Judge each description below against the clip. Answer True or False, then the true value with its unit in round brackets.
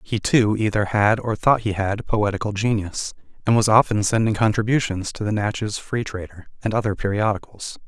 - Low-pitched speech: True (105 Hz)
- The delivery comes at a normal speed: True (175 wpm)